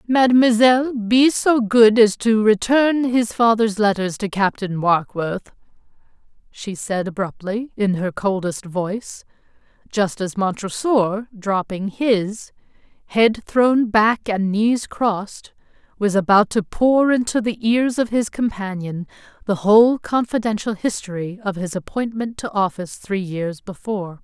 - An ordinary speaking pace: No, slow, 125 wpm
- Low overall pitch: No, high, 210 Hz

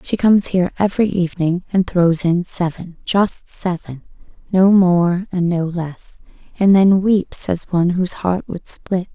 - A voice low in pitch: No, medium, 180 Hz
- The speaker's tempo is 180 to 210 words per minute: No, average, 150 wpm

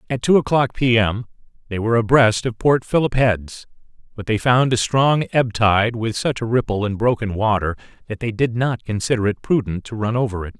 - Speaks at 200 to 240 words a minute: Yes, fast, 205 wpm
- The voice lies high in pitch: No, low, 115 Hz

